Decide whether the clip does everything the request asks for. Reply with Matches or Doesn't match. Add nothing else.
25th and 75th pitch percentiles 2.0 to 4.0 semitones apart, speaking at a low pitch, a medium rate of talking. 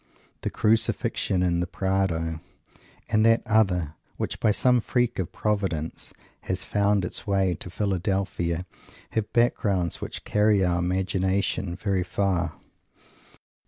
Doesn't match